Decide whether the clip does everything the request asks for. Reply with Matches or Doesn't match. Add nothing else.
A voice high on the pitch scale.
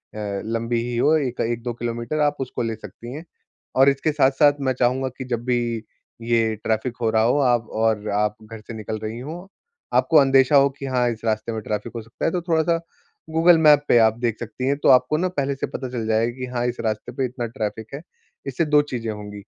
Doesn't match